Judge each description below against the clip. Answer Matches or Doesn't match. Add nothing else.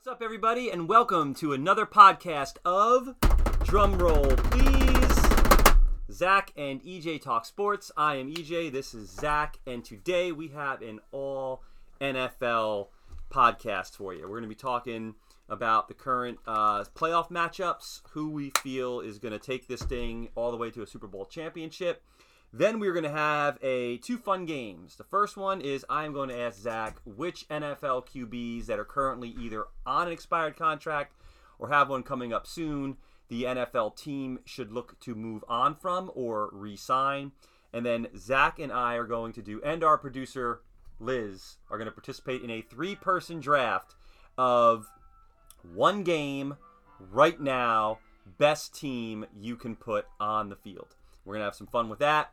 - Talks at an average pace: Matches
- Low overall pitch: Matches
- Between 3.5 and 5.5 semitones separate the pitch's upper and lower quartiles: Matches